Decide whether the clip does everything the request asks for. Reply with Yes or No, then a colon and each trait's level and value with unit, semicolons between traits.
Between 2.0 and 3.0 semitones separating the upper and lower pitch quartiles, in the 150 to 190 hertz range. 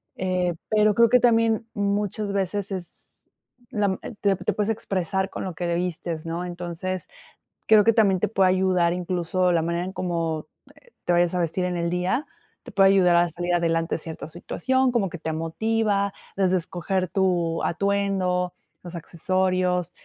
Yes: narrow, 2.5 semitones; medium, 185 Hz